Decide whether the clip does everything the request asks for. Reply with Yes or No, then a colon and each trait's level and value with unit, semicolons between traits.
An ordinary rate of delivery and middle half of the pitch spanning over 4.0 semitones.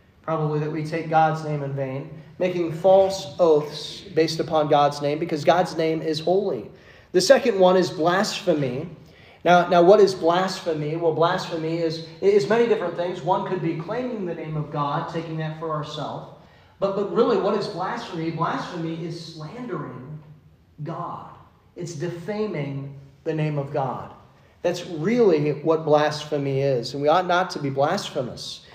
No: average, 160 wpm; average, 2.8 semitones